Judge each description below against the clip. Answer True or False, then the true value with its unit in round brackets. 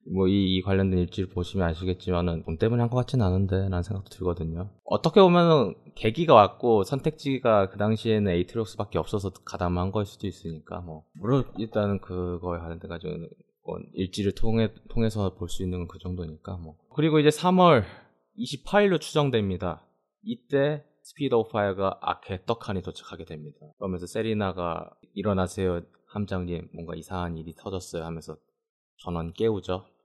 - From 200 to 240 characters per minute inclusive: False (360 characters per minute)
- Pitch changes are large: False (4.3 semitones)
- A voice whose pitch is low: True (95 Hz)